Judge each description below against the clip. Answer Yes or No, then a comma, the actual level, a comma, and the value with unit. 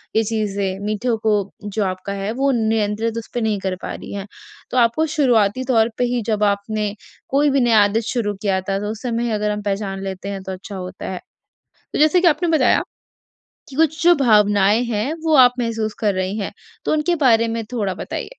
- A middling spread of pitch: Yes, average, 3.4 semitones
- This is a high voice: Yes, high, 215 Hz